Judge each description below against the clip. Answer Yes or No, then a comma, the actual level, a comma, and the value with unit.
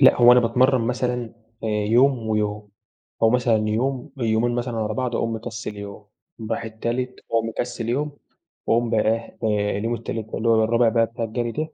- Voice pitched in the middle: No, low, 115 Hz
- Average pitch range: No, narrow, 1.8 semitones